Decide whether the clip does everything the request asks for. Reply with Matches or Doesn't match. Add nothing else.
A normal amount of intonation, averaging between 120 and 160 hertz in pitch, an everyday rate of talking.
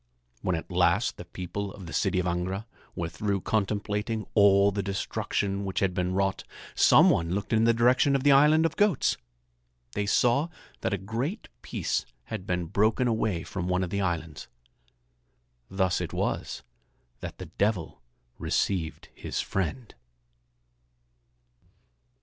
Doesn't match